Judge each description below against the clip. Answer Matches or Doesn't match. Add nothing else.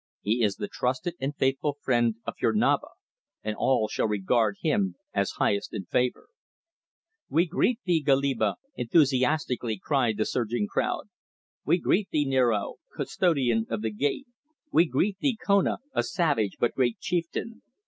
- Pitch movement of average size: Doesn't match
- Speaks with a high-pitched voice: Doesn't match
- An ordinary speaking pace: Matches